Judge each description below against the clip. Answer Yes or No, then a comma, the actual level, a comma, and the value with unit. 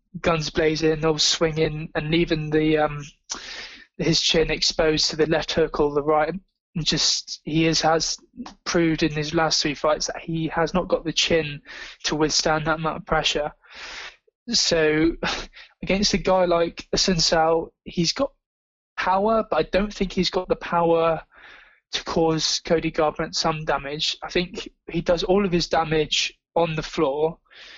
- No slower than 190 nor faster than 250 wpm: No, average, 160 wpm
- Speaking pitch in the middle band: Yes, medium, 160 Hz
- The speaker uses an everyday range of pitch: No, narrow, 2.0 semitones